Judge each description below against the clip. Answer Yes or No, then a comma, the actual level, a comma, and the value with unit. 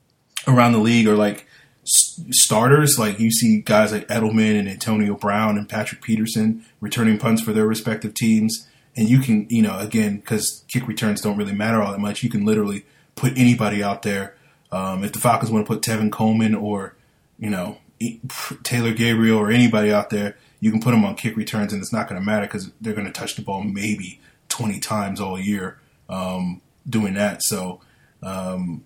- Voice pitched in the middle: No, low, 110 Hz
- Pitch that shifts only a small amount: Yes, narrow, 1.7 semitones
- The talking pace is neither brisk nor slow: Yes, average, 195 wpm